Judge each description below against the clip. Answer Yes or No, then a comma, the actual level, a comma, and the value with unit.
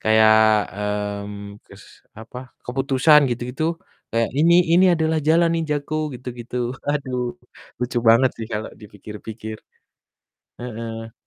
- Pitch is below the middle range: Yes, low, 125 Hz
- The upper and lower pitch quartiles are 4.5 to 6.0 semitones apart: Yes, average, 4.9 semitones